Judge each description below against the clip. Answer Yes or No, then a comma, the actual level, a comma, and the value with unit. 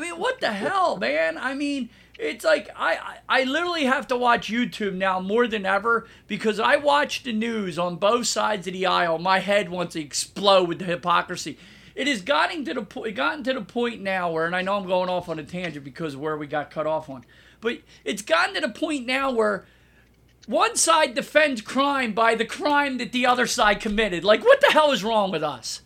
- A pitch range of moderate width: No, wide, 6.5 semitones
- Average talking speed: No, fast, 225 wpm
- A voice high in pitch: Yes, high, 220 Hz